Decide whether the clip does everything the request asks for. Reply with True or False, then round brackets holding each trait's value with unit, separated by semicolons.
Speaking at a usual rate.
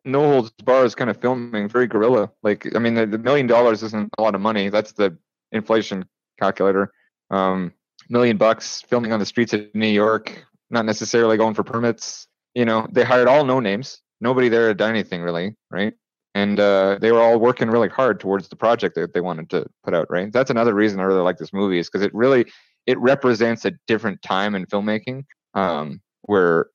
False (210 wpm)